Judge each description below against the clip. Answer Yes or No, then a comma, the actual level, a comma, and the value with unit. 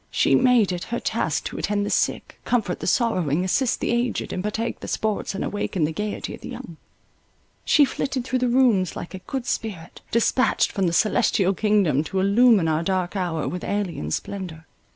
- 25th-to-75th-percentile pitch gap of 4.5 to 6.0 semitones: Yes, average, 4.8 semitones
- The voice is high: Yes, high, 200 Hz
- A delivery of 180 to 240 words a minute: Yes, average, 195 wpm